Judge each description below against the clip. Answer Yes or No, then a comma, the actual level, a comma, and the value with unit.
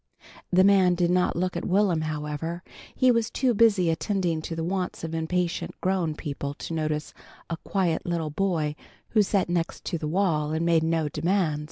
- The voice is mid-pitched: Yes, medium, 170 Hz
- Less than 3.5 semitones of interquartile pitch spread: Yes, average, 2.9 semitones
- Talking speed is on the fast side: No, average, 180 wpm